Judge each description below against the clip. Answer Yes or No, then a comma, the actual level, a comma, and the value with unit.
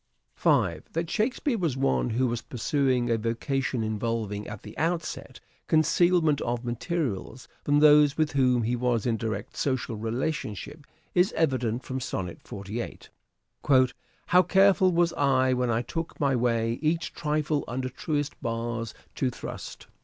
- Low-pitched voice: Yes, low, 130 Hz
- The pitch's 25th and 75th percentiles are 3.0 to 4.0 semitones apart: No, average, 4.8 semitones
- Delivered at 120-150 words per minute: Yes, average, 145 wpm